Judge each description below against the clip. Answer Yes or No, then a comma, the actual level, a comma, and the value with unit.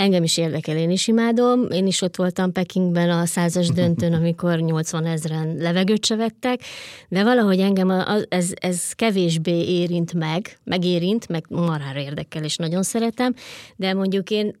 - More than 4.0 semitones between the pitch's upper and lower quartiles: No, narrow, 2.6 semitones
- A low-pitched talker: No, medium, 180 Hz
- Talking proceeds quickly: Yes, fast, 160 wpm